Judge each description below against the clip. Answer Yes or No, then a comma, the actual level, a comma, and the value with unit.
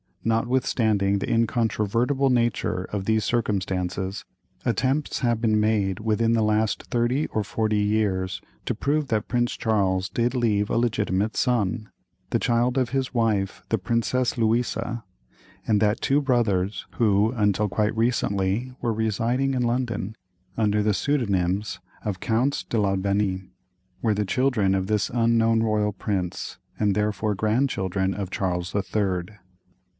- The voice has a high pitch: No, low, 110 Hz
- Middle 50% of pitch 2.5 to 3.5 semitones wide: Yes, average, 3.0 semitones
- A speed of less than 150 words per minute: Yes, average, 140 wpm